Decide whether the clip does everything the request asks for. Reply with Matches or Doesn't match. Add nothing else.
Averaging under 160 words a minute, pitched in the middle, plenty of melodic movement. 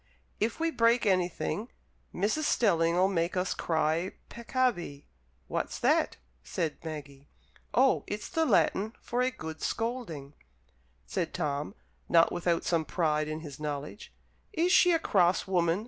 Matches